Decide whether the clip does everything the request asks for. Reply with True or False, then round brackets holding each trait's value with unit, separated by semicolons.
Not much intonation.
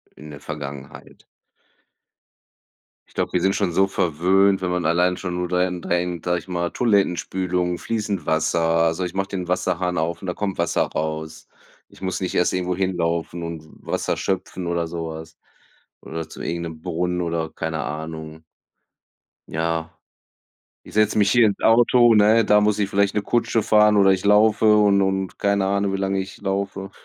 False (3.0 semitones)